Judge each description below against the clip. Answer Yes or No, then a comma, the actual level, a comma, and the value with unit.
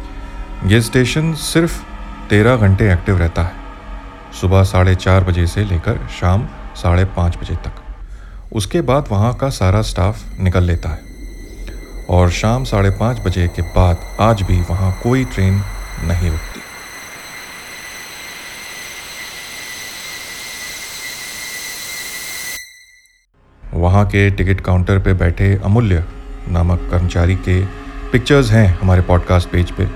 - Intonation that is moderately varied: Yes, average, 4.2 semitones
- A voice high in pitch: No, very low, 95 Hz